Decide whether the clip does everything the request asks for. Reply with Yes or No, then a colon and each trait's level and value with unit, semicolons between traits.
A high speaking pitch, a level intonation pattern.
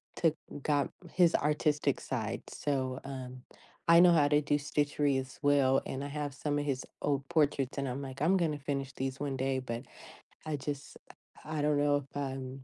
No: medium, 140 Hz; narrow, 1.8 semitones